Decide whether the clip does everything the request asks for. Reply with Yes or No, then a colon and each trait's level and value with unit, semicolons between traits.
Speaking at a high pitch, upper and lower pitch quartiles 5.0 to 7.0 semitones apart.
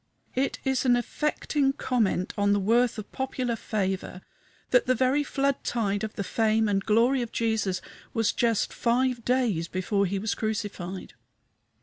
No: high, 225 Hz; average, 4.0 semitones